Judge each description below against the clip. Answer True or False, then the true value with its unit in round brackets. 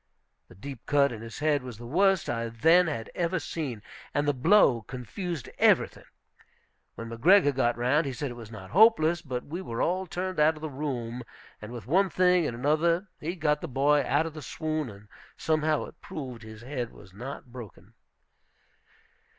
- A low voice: False (145 Hz)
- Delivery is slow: False (190 wpm)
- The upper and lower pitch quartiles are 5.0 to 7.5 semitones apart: True (5.3 semitones)